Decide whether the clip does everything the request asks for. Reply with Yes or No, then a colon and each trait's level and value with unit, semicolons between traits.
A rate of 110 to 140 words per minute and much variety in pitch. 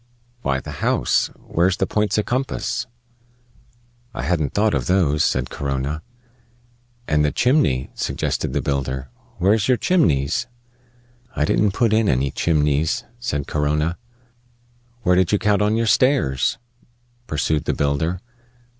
Yes: slow, 135 wpm; wide, 6.9 semitones